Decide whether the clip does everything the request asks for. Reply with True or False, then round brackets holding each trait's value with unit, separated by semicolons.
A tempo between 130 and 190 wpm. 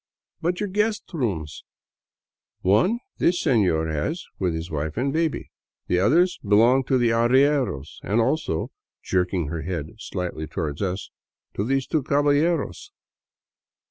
True (155 wpm)